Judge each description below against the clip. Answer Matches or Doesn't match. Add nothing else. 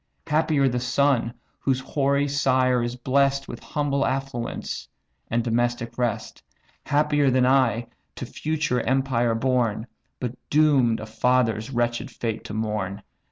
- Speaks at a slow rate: Matches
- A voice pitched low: Matches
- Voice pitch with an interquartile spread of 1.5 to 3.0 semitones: Matches